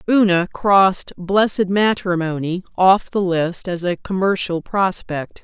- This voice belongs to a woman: Yes, female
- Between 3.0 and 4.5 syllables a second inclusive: Yes, 4.0 syllables/s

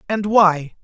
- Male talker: Yes, male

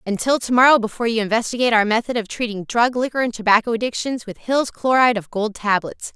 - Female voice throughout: Yes, female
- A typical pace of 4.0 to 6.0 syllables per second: No, 6.5 syllables/s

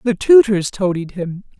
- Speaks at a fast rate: No, average, 150 wpm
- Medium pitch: No, high, 195 Hz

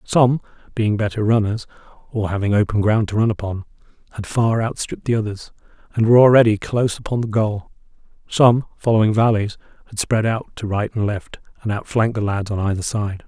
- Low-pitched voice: Yes, low, 110 Hz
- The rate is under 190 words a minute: Yes, average, 180 wpm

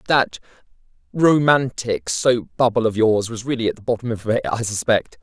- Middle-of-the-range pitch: No, low, 115 Hz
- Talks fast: No, average, 170 wpm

